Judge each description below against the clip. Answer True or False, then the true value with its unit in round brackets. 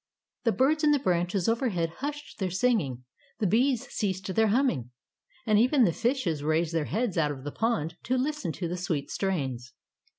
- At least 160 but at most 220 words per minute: True (185 wpm)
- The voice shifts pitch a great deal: True (7.1 semitones)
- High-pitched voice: True (195 Hz)